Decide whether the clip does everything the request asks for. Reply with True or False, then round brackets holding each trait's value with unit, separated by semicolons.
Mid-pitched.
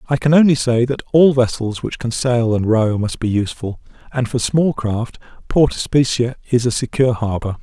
False (120 Hz)